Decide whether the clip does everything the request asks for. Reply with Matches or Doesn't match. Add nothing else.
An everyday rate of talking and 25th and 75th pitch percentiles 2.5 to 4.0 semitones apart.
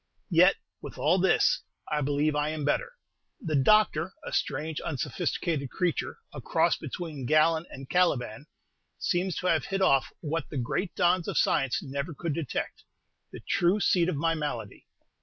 Matches